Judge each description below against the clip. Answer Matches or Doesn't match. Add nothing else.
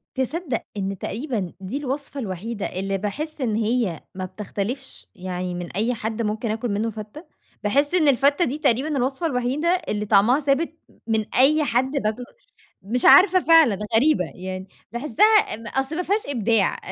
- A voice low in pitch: Doesn't match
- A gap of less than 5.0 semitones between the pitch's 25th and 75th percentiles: Doesn't match